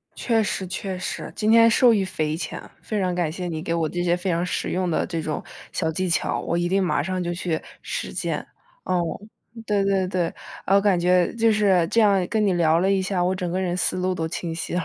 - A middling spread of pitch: No, narrow, 2.3 semitones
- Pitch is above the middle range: No, medium, 180 Hz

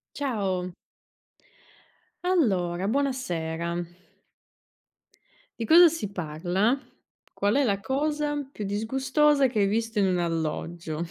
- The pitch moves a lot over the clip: Yes, wide, 7.6 semitones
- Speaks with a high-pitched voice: Yes, high, 205 Hz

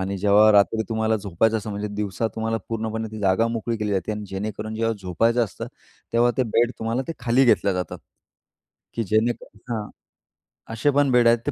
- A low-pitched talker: Yes, low, 110 Hz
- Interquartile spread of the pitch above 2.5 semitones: No, narrow, 2.0 semitones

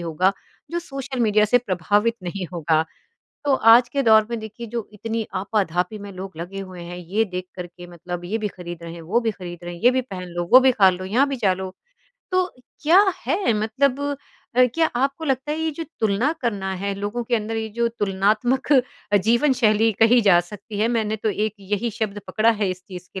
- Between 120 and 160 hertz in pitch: No, high, 215 Hz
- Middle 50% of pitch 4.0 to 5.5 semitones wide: Yes, average, 4.4 semitones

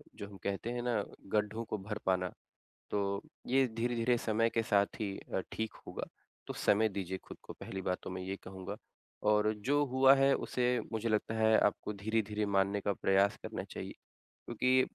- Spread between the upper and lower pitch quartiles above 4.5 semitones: No, narrow, 2.6 semitones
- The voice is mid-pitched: No, low, 105 Hz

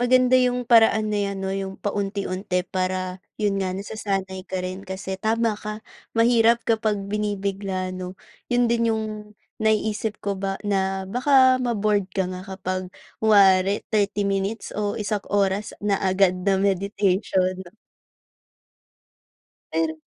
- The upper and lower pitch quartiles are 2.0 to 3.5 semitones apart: Yes, narrow, 2.4 semitones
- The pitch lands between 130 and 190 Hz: No, high, 200 Hz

